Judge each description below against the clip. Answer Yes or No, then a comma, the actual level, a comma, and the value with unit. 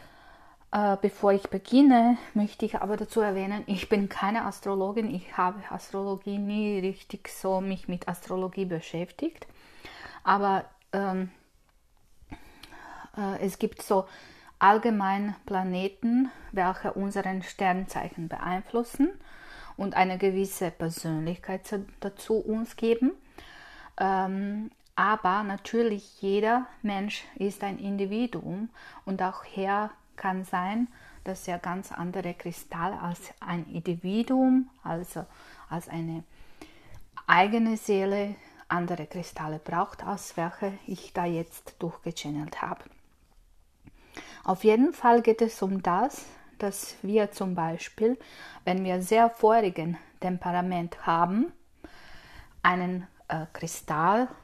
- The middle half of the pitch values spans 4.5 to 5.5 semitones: No, average, 3.2 semitones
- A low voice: No, high, 195 Hz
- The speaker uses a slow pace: Yes, slow, 110 wpm